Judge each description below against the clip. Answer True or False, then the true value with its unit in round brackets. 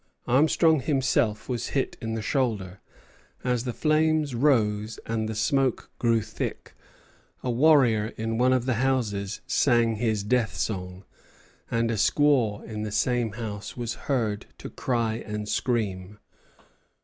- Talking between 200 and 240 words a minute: False (140 wpm)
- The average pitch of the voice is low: True (115 Hz)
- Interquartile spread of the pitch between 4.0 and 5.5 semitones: False (3.3 semitones)